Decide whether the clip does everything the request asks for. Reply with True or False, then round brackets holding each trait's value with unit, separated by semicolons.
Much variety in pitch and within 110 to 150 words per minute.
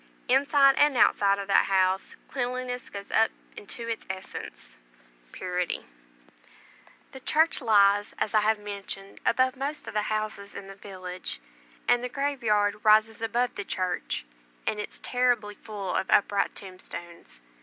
False (3.9 semitones; 145 wpm)